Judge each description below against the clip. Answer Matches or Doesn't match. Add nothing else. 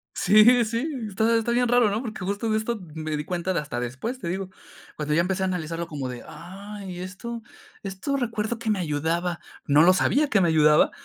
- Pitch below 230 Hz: Matches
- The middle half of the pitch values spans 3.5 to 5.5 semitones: Matches